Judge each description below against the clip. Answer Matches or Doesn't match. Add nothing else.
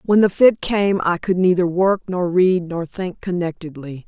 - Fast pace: Doesn't match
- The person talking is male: Doesn't match